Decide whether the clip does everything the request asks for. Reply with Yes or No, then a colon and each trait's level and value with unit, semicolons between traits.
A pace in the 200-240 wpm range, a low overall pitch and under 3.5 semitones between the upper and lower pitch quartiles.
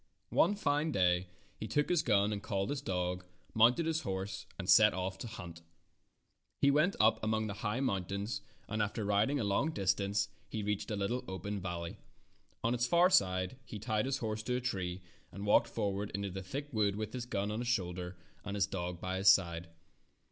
No: fast, 205 wpm; low, 105 Hz; average, 3.9 semitones